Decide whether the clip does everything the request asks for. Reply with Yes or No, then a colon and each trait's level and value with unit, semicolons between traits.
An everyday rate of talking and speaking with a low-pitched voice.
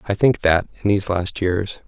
No: fast, 225 wpm; very low, 95 Hz